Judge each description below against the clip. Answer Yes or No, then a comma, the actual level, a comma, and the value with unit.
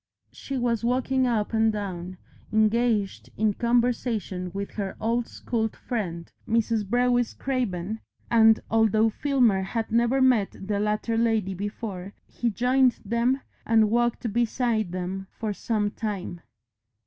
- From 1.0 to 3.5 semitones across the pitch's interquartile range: Yes, average, 2.9 semitones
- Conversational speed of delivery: No, slow, 130 wpm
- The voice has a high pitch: Yes, high, 225 Hz